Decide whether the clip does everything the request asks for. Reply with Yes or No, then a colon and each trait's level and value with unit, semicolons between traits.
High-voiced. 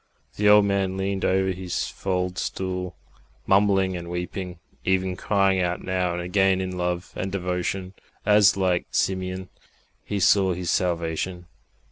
No: very low, 95 Hz